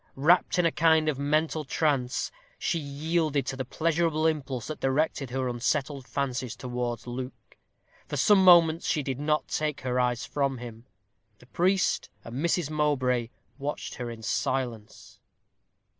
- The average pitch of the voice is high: No, medium, 140 Hz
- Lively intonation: No, average, 3.8 semitones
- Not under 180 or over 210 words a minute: No, average, 150 wpm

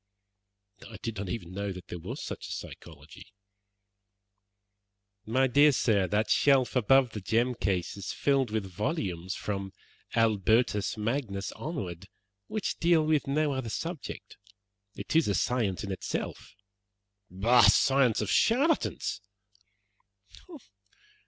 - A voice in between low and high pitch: No, low, 115 Hz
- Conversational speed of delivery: No, slow, 125 wpm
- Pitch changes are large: Yes, wide, 5.7 semitones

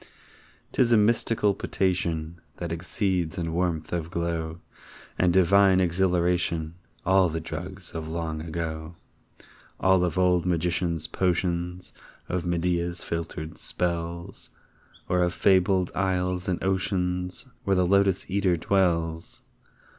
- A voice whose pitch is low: Yes, very low, 90 Hz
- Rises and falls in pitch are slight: Yes, narrow, 1.9 semitones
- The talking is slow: Yes, slow, 115 wpm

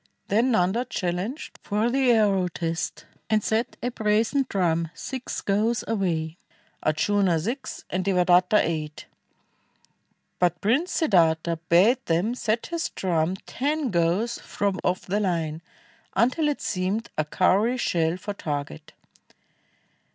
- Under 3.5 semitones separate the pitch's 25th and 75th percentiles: No, average, 5.2 semitones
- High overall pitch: Yes, high, 195 Hz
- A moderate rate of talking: No, slow, 125 wpm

